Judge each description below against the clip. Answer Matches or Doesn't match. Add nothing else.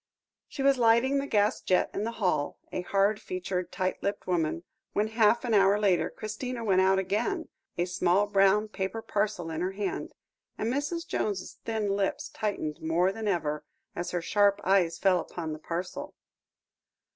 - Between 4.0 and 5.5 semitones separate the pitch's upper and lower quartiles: Doesn't match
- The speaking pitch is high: Matches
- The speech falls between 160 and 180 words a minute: Matches